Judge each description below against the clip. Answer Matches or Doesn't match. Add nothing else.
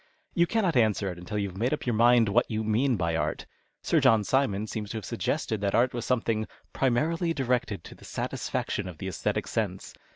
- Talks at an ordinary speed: Doesn't match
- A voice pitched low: Matches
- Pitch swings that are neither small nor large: Matches